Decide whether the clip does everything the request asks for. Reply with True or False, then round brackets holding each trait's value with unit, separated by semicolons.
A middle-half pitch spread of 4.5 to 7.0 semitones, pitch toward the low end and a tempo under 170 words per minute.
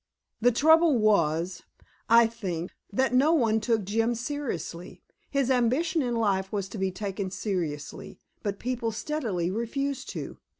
False (5.0 semitones; 225 Hz; 140 wpm)